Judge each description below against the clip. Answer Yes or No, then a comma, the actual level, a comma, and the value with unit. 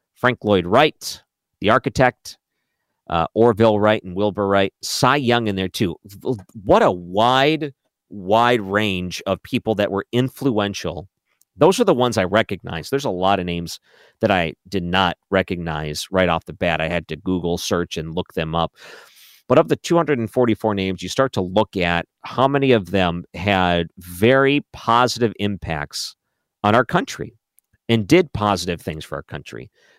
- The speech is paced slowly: No, average, 165 wpm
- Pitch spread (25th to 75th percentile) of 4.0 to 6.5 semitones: Yes, average, 5.1 semitones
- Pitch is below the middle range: Yes, low, 100 Hz